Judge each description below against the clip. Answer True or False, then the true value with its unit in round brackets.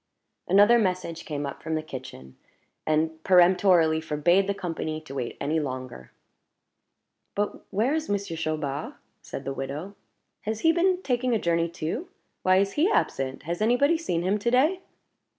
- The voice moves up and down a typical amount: False (5.7 semitones)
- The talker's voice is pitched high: False (175 Hz)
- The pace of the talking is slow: False (165 wpm)